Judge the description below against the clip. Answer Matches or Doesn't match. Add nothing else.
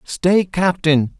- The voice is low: Doesn't match